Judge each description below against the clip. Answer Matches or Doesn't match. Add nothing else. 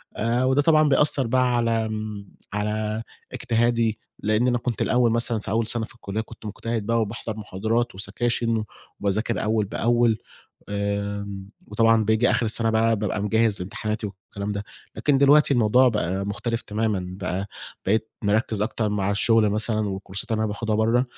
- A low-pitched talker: Matches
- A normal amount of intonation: Doesn't match